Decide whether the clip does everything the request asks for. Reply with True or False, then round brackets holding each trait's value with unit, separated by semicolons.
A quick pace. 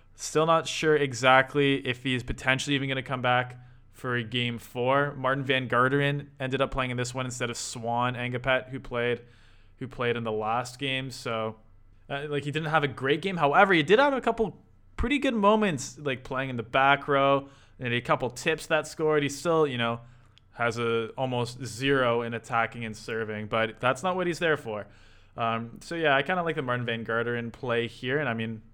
True (215 wpm)